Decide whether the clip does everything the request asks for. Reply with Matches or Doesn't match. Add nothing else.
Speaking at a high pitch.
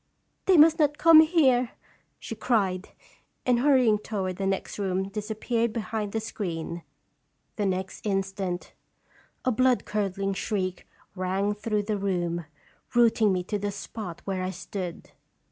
Matches